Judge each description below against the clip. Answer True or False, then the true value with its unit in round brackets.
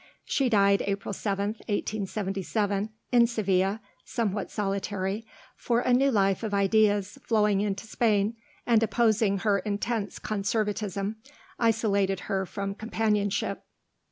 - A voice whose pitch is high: True (205 Hz)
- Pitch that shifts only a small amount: True (2.0 semitones)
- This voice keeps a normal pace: False (115 wpm)